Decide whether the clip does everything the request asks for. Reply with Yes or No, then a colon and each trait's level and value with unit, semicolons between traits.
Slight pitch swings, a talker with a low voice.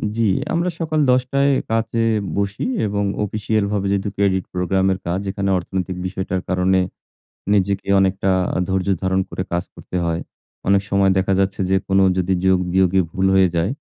Yes: narrow, 1.3 semitones; very low, 95 Hz